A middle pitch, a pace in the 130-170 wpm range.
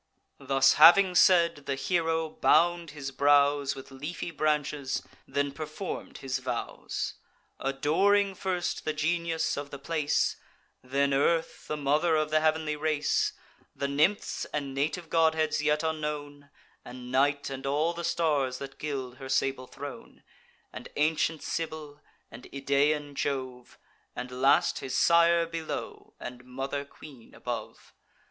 Yes: medium, 145 Hz; slow, 135 wpm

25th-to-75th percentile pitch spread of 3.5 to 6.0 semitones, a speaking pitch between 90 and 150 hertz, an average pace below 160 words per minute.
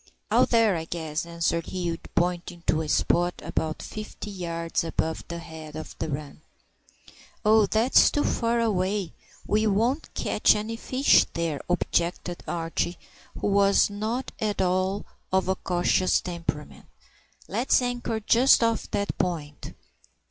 No: average, 4.3 semitones; medium, 185 Hz; average, 140 wpm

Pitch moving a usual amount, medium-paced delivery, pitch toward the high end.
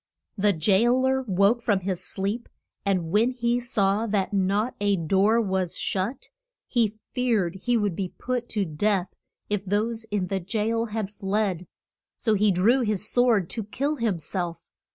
Yes: average, 3.3 semitones; average, 165 wpm; high, 205 Hz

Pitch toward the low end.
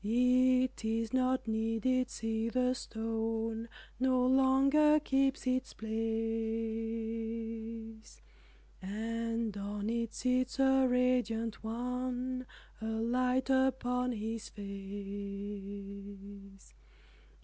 No: high, 230 Hz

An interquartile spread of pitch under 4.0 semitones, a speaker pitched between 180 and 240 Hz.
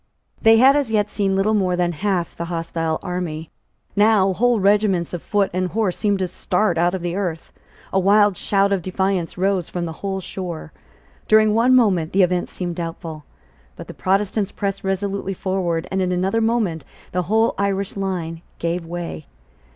Yes: average, 2.7 semitones; high, 190 Hz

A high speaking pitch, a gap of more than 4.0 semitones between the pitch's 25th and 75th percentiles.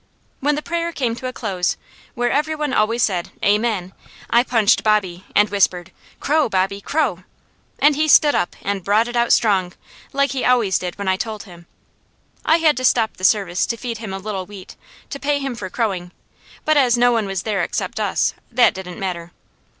Yes: high, 220 Hz; average, 5.0 semitones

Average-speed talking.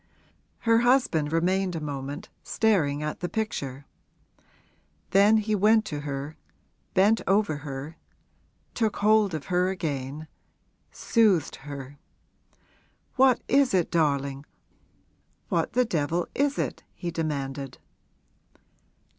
No: slow, 110 wpm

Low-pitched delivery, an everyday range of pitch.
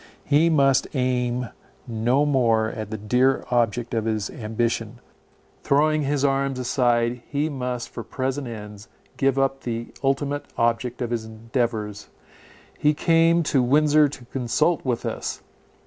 Yes: low, 125 Hz; average, 3.1 semitones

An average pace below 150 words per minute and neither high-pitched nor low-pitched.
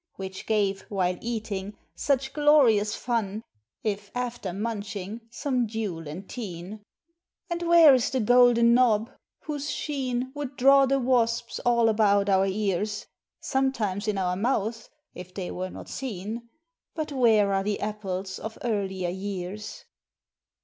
No: slow, 135 wpm; high, 215 Hz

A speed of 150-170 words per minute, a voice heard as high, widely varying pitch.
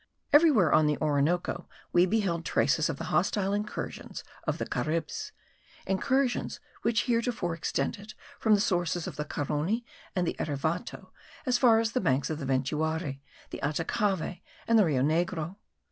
No: average, 155 wpm; medium, 175 Hz; wide, 5.7 semitones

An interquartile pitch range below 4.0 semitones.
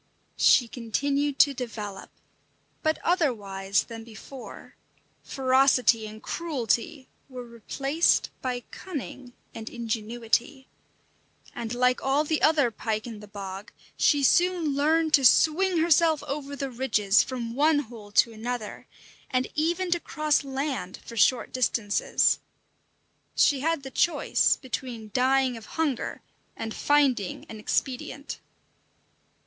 No: average, 4.3 semitones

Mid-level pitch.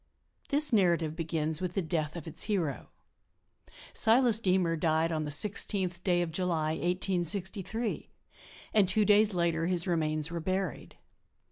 Yes: medium, 175 Hz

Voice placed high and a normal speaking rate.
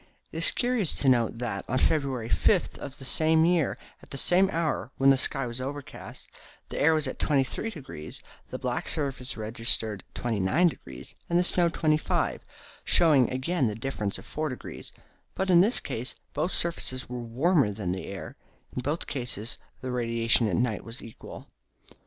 No: low, 135 Hz; average, 170 wpm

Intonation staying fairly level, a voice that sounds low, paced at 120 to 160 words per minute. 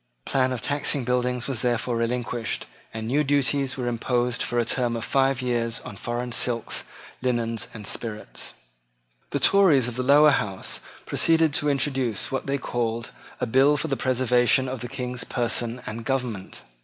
No: narrow, 2.3 semitones; low, 125 Hz; average, 170 wpm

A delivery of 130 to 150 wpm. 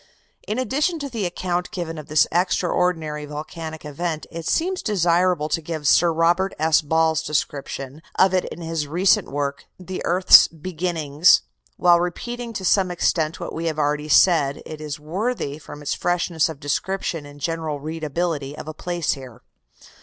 No: average, 165 wpm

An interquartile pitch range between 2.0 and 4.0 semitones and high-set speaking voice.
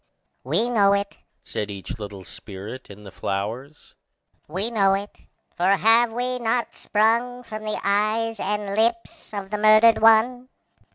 No: average, 4.5 semitones; high, 210 Hz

